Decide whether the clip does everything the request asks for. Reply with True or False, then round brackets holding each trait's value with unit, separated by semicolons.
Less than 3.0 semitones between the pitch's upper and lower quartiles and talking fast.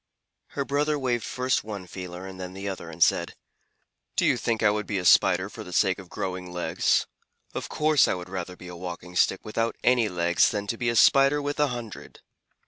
False (4.9 semitones; 210 wpm)